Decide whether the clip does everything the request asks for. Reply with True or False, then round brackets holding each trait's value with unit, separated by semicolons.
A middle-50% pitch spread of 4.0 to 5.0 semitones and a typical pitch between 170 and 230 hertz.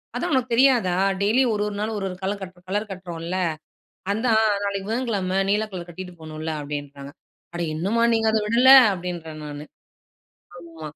True (4.7 semitones; 190 Hz)